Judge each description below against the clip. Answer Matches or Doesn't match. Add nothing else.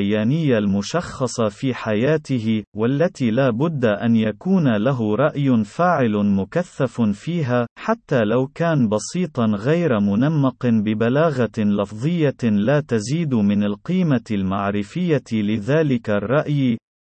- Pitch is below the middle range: Matches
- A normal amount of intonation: Doesn't match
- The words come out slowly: Doesn't match